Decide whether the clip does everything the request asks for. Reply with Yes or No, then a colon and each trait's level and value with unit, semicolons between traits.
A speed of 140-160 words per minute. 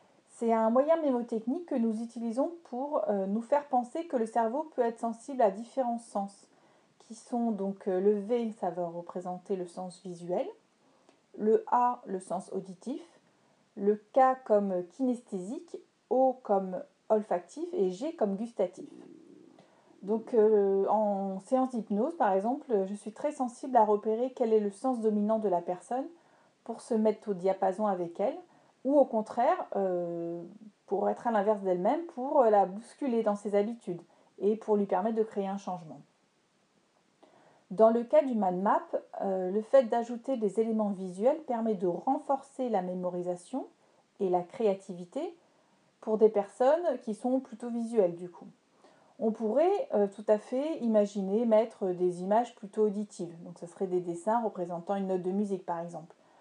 Yes: average, 155 wpm